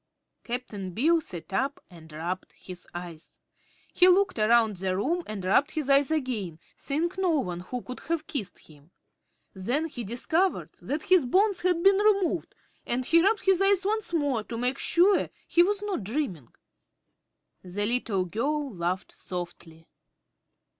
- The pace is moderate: Yes, average, 155 wpm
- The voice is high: Yes, very high, 255 Hz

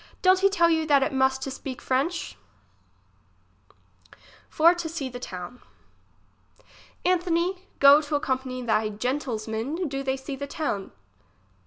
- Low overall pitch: No, very high, 275 Hz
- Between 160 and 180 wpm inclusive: No, average, 140 wpm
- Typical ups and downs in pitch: Yes, average, 4.5 semitones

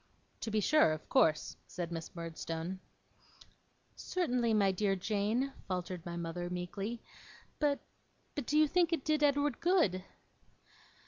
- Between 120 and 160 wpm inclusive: Yes, slow, 135 wpm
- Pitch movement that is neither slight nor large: No, wide, 8.3 semitones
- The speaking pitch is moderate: No, high, 205 Hz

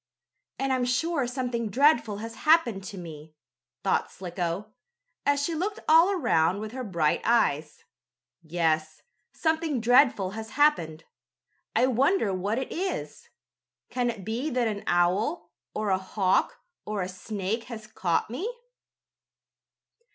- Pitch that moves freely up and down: Yes, wide, 6.2 semitones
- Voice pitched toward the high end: Yes, high, 220 Hz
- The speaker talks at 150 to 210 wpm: No, slow, 135 wpm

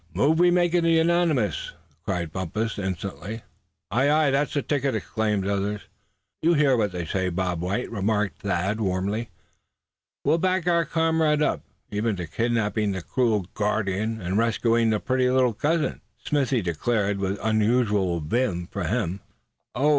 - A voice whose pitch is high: No, low, 110 Hz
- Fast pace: No, average, 150 wpm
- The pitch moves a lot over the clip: Yes, wide, 6.0 semitones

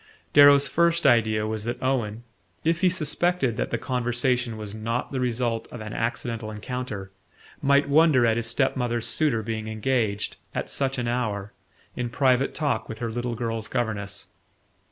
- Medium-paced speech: Yes, average, 165 wpm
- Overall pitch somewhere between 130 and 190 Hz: No, low, 120 Hz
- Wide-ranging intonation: No, average, 3.2 semitones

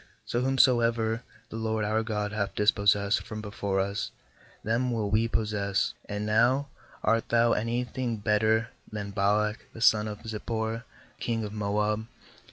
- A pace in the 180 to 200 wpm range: No, average, 150 wpm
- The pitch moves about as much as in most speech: No, narrow, 1.7 semitones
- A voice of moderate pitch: No, low, 110 Hz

